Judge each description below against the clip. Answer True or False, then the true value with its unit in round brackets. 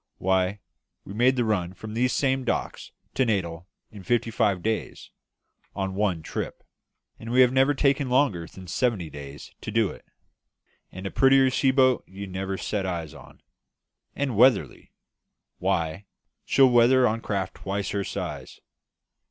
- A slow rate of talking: False (155 wpm)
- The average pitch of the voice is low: True (105 Hz)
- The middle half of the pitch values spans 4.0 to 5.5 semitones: True (5.2 semitones)